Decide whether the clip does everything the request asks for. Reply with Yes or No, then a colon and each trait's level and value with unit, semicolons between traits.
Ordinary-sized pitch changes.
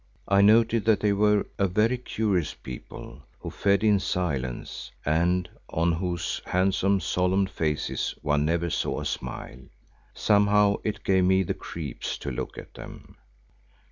Yes: average, 3.5 semitones